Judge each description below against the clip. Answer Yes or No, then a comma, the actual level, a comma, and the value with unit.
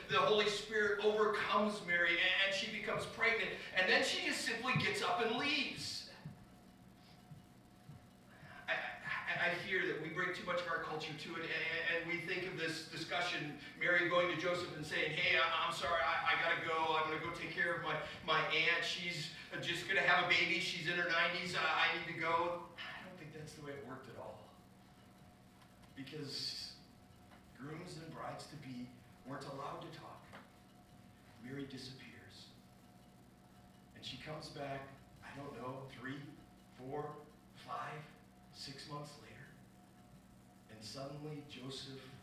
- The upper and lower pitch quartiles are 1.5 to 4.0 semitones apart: No, wide, 5.4 semitones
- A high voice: No, medium, 155 Hz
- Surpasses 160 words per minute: No, average, 155 wpm